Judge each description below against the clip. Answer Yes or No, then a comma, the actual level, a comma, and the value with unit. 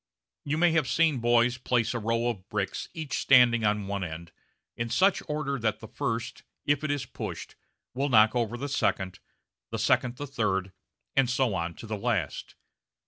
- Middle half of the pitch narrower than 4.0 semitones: No, average, 4.6 semitones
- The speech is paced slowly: No, average, 185 wpm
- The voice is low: Yes, low, 120 Hz